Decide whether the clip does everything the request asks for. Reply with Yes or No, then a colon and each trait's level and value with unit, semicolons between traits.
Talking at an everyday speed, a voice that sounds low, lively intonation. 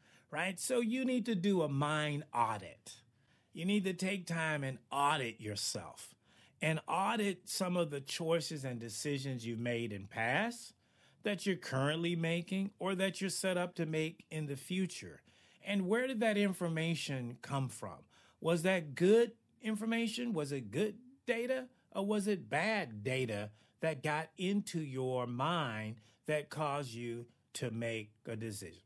No: average, 155 wpm; medium, 155 Hz; wide, 7.5 semitones